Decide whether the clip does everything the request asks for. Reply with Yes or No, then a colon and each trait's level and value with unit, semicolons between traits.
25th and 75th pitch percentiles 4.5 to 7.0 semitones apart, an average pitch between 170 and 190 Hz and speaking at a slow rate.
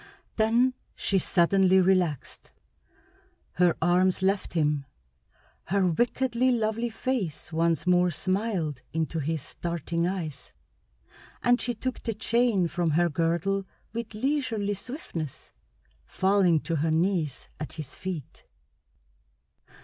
Yes: average, 4.9 semitones; medium, 185 Hz; slow, 110 wpm